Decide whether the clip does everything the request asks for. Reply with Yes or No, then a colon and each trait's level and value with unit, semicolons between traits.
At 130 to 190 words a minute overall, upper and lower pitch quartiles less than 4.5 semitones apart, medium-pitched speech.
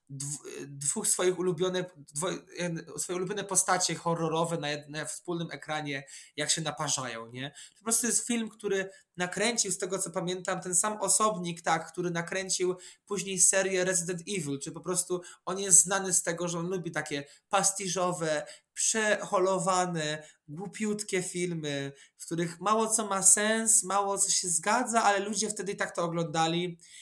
Yes: average, 145 wpm; average, 2.9 semitones; medium, 180 Hz